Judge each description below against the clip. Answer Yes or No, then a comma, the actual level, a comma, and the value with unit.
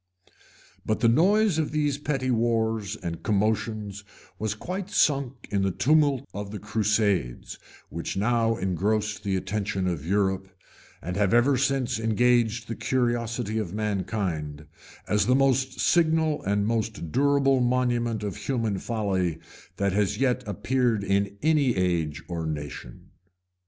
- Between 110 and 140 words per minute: Yes, slow, 135 wpm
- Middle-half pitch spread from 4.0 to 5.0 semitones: Yes, average, 4.4 semitones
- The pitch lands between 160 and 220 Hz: No, low, 110 Hz